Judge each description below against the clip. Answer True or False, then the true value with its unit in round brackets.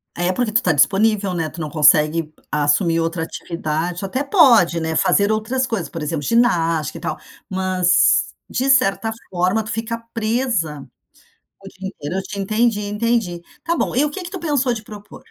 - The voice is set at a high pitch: True (195 Hz)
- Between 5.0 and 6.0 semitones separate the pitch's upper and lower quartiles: True (5.6 semitones)